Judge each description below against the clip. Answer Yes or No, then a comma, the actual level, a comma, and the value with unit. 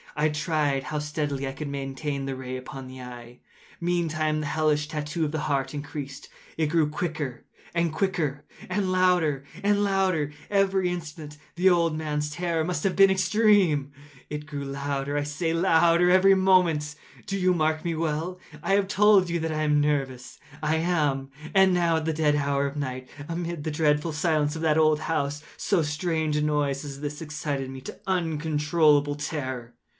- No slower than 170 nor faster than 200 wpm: Yes, average, 180 wpm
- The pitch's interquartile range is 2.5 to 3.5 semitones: Yes, average, 2.8 semitones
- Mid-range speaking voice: Yes, medium, 155 Hz